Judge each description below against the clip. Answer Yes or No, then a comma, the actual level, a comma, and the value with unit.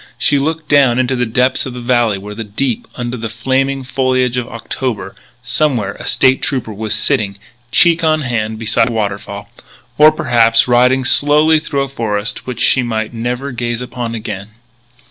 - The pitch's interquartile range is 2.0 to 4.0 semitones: Yes, average, 3.0 semitones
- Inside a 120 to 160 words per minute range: No, average, 170 wpm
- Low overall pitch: Yes, low, 125 Hz